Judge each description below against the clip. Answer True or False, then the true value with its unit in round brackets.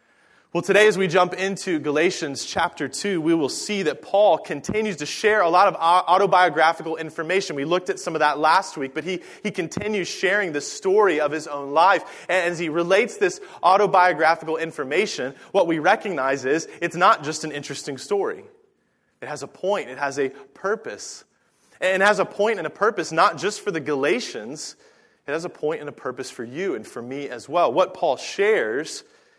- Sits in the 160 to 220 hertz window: True (185 Hz)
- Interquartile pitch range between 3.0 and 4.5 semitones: False (4.9 semitones)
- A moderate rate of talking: True (195 wpm)